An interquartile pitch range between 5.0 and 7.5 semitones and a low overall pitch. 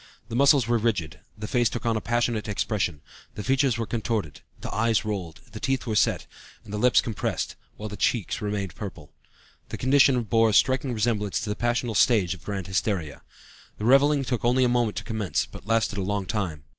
No: average, 2.9 semitones; low, 110 Hz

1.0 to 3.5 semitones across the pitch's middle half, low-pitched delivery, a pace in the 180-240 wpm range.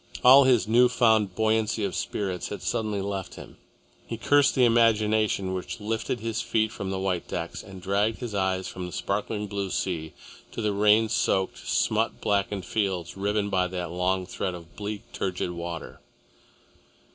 No: average, 2.8 semitones; low, 100 Hz; average, 170 wpm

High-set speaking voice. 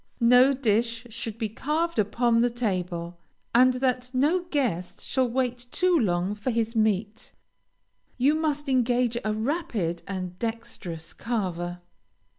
Yes: high, 235 Hz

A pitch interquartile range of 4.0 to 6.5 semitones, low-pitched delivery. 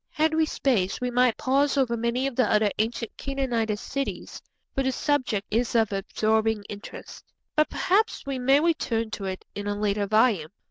No: average, 4.3 semitones; high, 235 Hz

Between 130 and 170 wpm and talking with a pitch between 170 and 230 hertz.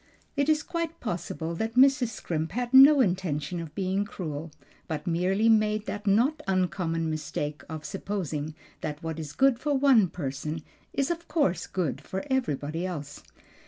Yes: average, 160 wpm; medium, 185 Hz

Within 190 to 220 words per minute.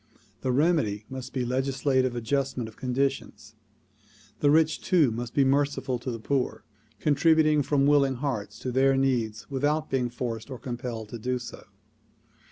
No: average, 160 wpm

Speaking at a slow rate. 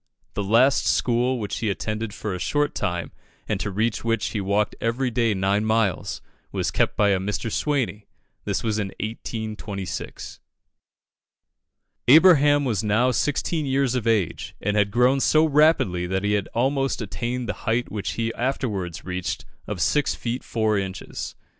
No: average, 160 wpm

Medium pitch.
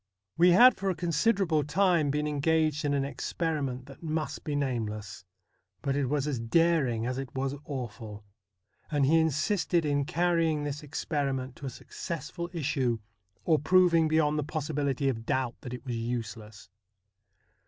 Yes: medium, 145 Hz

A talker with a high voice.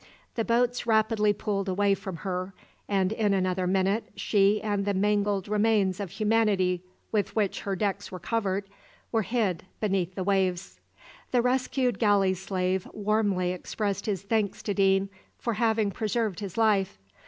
Yes: high, 200 Hz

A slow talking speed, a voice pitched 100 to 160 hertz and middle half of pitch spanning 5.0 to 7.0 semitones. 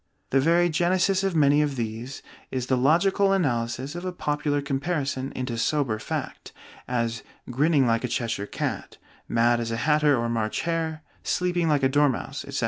No: average, 170 wpm; medium, 140 Hz; average, 5.3 semitones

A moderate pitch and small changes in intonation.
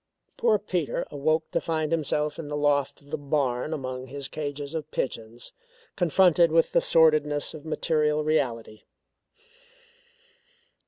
Yes: medium, 150 Hz; narrow, 2.0 semitones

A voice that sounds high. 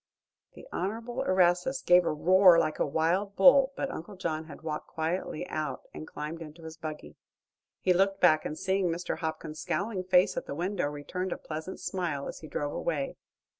No: medium, 175 Hz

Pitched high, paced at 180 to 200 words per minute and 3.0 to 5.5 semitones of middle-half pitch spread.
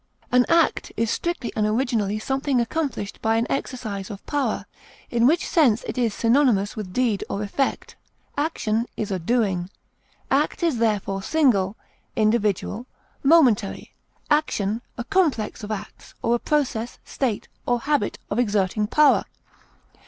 No: high, 230 Hz; average, 145 wpm; average, 4.6 semitones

